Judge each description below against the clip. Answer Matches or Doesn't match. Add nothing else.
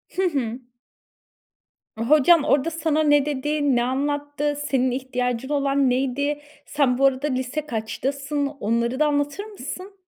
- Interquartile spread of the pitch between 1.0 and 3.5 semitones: Matches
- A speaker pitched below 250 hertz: Doesn't match